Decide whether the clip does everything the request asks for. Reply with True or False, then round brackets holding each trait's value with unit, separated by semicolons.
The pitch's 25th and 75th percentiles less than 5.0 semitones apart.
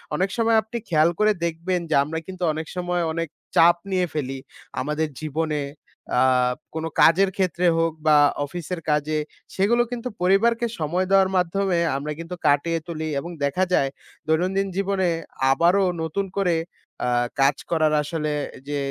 True (3.5 semitones)